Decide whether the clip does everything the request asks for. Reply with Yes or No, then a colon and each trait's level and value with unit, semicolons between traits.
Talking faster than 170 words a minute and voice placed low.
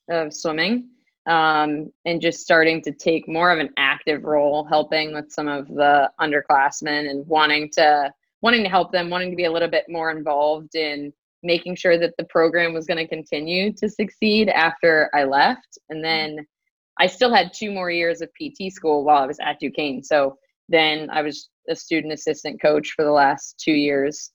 No: average, 190 wpm; medium, 160 Hz